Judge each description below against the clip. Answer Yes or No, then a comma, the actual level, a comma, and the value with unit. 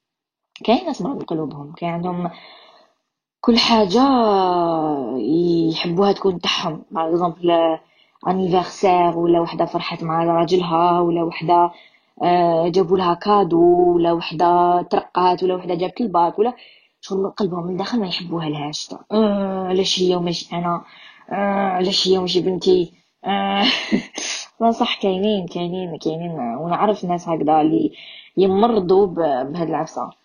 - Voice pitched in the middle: Yes, medium, 175 Hz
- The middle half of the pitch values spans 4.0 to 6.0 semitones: No, narrow, 2.4 semitones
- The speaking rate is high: No, average, 125 wpm